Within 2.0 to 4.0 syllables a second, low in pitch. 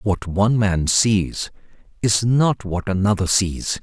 Yes: 3.7 syllables/s; low, 100 Hz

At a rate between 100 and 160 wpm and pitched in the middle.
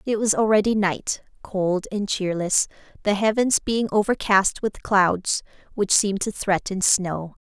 No: average, 145 wpm; high, 200 Hz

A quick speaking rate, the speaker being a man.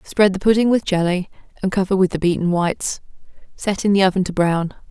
No: fast, 210 wpm; female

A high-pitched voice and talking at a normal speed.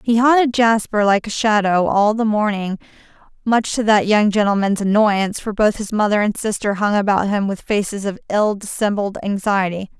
Yes: high, 210 Hz; average, 180 wpm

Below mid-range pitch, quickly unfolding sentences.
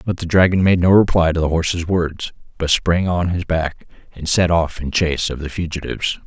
Yes: very low, 85 Hz; fast, 220 wpm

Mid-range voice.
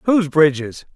Yes: medium, 160 Hz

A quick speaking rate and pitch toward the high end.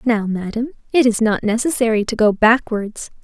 No: average, 165 wpm; high, 225 Hz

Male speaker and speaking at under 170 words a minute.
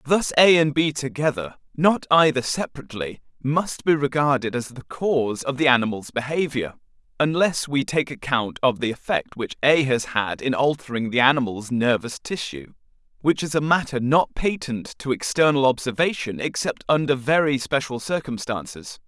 Yes: male; average, 155 wpm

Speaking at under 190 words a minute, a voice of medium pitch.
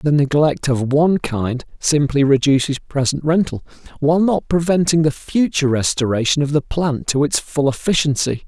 Yes: average, 155 wpm; medium, 145 Hz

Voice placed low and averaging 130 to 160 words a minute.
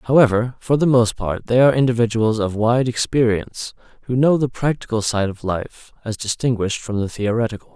No: low, 115 Hz; average, 180 wpm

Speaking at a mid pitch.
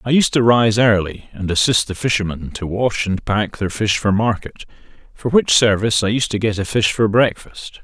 No: low, 110 Hz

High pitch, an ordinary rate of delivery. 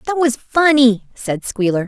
Yes: very high, 250 Hz; average, 160 wpm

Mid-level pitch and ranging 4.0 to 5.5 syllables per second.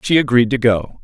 No: low, 120 Hz; 5.4 syllables/s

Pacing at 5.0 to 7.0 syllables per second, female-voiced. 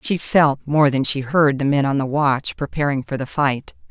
No: 4.7 syllables/s; female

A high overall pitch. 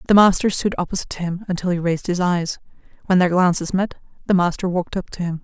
No: medium, 180 Hz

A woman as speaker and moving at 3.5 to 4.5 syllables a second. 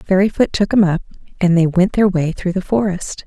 No: female; 5.4 syllables/s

